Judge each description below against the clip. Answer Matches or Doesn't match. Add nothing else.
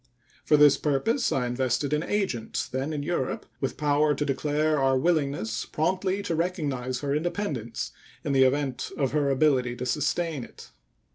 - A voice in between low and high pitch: Matches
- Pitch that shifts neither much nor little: Matches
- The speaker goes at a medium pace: Matches